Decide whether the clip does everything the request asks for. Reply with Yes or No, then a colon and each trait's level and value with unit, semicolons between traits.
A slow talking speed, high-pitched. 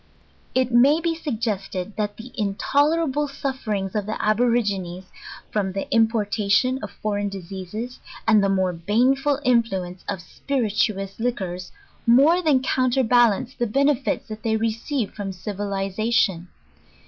Yes: slow, 125 wpm; high, 220 Hz